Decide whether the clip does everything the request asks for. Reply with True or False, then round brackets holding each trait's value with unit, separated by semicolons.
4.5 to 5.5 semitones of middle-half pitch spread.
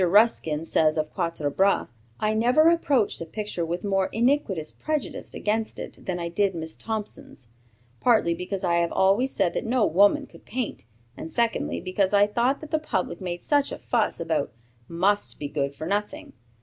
True (5.2 semitones)